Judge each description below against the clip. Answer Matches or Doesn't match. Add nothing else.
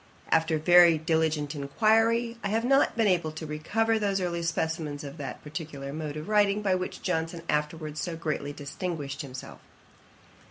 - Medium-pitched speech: Matches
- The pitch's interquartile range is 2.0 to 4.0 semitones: Doesn't match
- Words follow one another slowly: Doesn't match